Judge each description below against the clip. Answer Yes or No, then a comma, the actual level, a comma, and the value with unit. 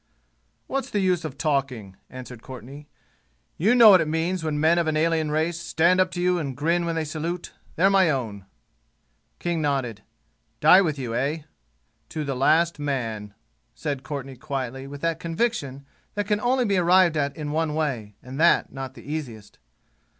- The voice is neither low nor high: Yes, medium, 155 Hz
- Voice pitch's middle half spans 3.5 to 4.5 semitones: Yes, average, 4.2 semitones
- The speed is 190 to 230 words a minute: No, average, 180 wpm